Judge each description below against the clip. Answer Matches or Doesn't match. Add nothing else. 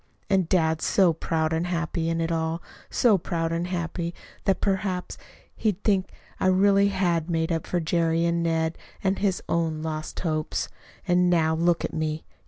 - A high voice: Doesn't match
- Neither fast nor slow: Matches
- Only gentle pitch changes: Matches